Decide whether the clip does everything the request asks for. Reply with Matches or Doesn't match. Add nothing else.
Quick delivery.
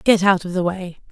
Matches